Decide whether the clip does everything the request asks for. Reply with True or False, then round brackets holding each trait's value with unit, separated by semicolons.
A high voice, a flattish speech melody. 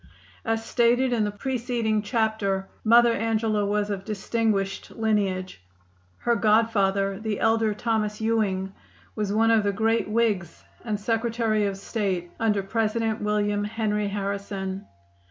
True (215 Hz; 2.0 semitones)